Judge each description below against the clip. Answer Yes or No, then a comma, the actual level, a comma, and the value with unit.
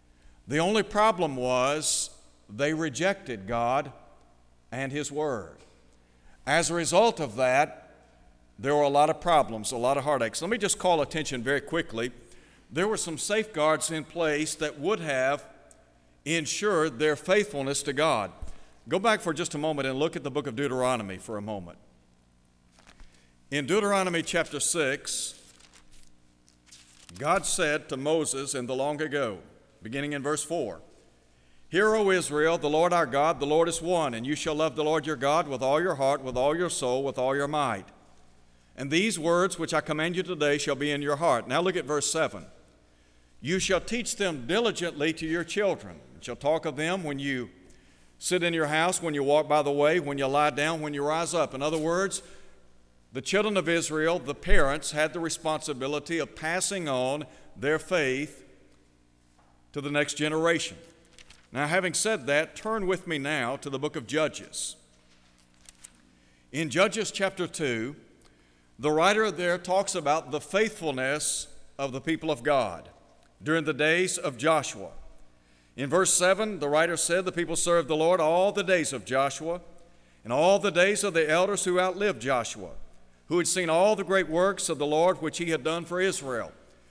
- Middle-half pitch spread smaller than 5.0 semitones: No, average, 5.3 semitones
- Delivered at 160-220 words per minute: Yes, average, 175 wpm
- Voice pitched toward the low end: No, medium, 150 Hz